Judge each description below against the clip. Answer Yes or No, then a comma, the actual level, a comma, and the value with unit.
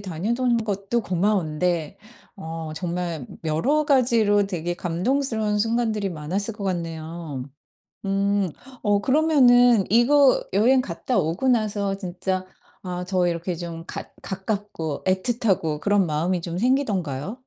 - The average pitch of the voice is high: Yes, high, 195 Hz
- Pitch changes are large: No, average, 4.8 semitones